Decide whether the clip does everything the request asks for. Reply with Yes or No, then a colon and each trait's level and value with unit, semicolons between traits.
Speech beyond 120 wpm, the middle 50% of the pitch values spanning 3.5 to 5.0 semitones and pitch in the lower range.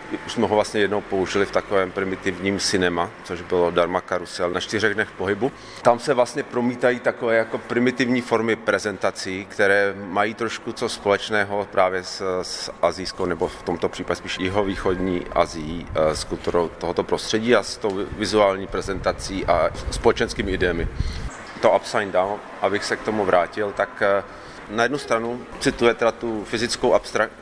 Yes: average, 160 wpm; average, 3.8 semitones; low, 100 Hz